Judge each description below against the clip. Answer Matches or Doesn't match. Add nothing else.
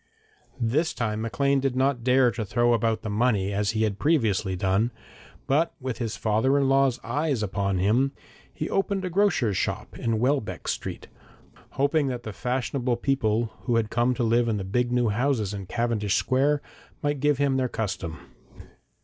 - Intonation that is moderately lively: Matches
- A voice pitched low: Matches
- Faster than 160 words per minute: Matches